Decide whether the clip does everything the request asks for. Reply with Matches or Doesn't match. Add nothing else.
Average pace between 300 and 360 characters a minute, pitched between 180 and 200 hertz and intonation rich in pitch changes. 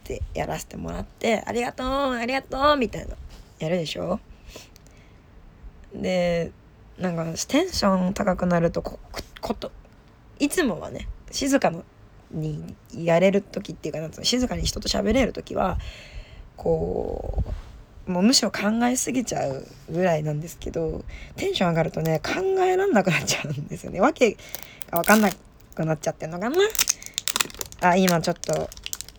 Matches